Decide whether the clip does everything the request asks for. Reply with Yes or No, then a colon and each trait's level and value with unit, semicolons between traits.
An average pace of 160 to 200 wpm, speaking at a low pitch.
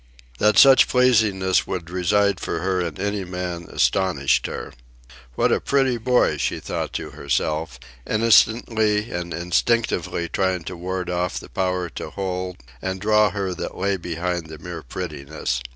No: average, 150 wpm; very low, 95 Hz